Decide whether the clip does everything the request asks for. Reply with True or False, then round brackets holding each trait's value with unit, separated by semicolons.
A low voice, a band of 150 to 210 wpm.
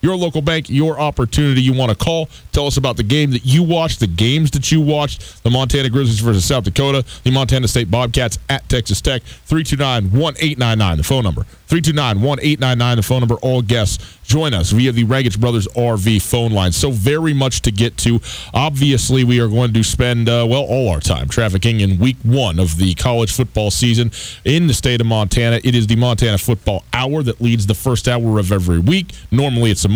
True (120 Hz; 205 wpm)